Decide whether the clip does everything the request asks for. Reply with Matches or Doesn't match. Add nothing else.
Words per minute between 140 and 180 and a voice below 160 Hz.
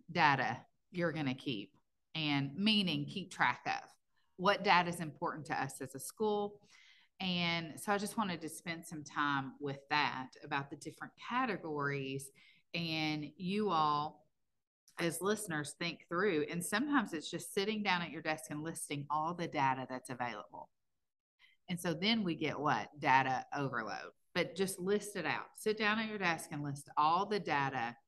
Doesn't match